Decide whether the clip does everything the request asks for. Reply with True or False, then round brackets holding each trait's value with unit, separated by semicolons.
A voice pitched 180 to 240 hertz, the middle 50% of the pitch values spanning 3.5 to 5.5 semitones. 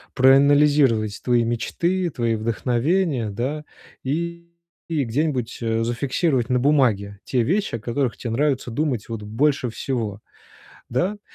False (130 Hz; 4.6 semitones)